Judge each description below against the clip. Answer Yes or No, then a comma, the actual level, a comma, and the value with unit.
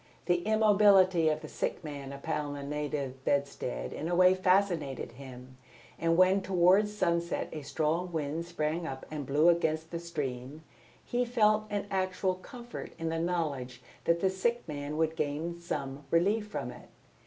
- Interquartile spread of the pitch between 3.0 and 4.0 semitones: No, average, 4.4 semitones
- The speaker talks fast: No, average, 165 wpm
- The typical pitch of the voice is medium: Yes, medium, 165 Hz